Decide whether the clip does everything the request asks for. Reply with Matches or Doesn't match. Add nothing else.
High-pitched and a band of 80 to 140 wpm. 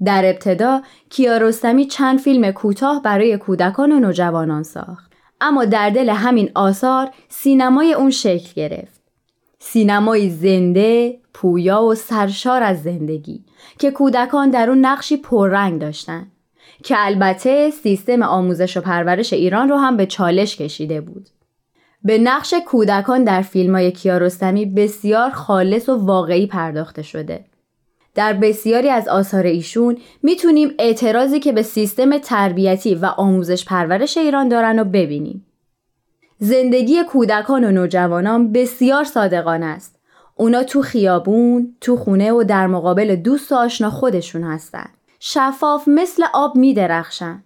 Matches